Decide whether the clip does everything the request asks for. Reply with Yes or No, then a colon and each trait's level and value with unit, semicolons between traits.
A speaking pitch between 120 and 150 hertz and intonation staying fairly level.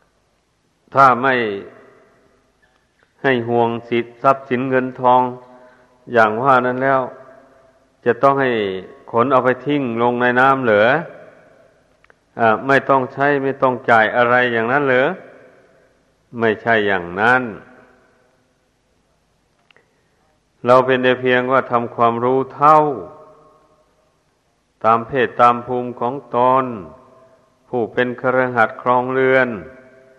Yes: low, 125 Hz; narrow, 1.5 semitones